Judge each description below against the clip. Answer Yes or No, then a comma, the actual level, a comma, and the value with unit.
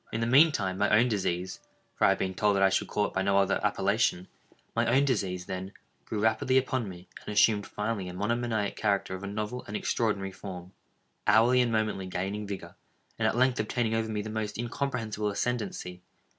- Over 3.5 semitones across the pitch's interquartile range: No, average, 3.0 semitones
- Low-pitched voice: Yes, low, 105 Hz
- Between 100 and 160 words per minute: No, average, 190 wpm